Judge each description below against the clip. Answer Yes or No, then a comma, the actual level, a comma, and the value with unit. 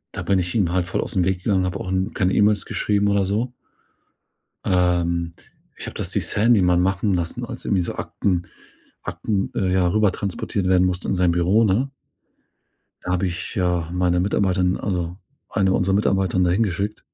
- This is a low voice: Yes, very low, 95 Hz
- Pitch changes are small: Yes, narrow, 1.9 semitones